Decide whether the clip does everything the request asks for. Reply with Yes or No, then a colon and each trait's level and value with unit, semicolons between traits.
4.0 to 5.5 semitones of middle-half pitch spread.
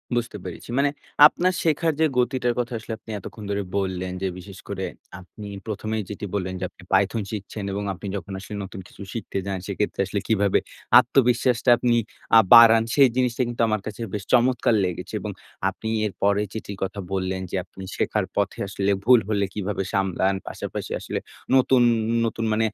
No: average, 3.6 semitones